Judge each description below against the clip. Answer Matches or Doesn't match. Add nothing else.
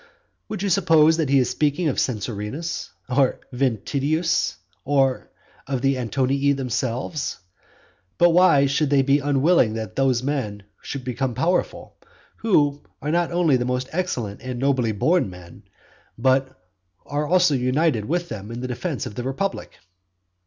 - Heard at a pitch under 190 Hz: Matches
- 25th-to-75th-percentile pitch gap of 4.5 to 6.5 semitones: Doesn't match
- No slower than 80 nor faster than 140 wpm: Doesn't match